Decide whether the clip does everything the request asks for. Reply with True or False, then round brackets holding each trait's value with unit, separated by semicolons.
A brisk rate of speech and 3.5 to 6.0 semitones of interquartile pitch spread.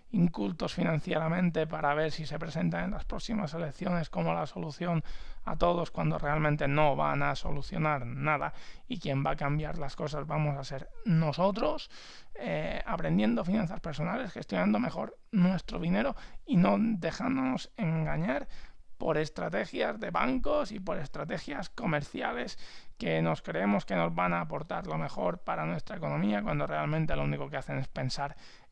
False (155 wpm; 4.2 semitones)